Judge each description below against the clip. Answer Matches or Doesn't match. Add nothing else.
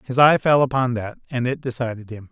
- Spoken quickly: Matches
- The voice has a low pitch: Matches